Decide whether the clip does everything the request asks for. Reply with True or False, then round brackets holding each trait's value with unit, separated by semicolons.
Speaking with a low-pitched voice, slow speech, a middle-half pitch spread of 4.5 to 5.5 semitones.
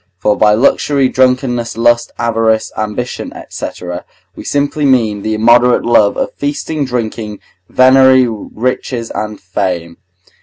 False (120 Hz; 120 wpm; 3.1 semitones)